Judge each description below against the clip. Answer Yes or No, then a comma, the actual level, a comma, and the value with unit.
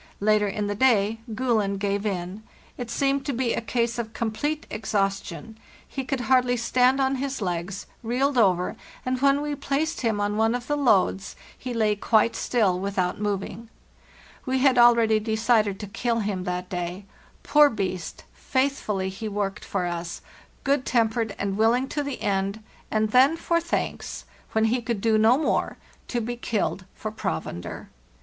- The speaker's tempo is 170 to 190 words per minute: Yes, average, 175 wpm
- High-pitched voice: Yes, high, 220 Hz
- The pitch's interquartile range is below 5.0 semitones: Yes, average, 4.1 semitones